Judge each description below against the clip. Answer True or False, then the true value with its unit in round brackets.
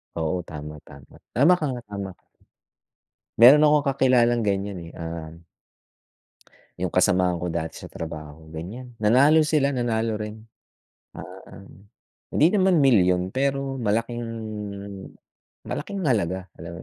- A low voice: True (105 Hz)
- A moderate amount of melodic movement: False (6.9 semitones)